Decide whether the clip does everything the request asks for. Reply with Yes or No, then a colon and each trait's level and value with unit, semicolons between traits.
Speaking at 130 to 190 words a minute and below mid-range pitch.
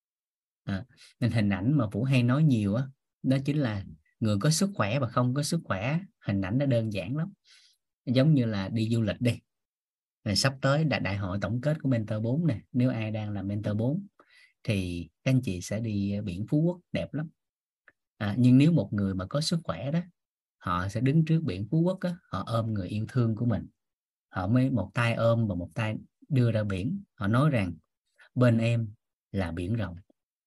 No: average, 215 wpm; low, 120 Hz